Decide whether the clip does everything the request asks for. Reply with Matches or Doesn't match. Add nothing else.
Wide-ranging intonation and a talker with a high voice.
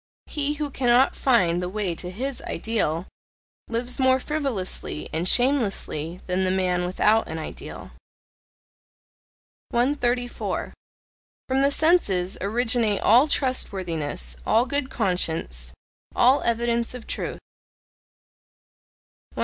Matches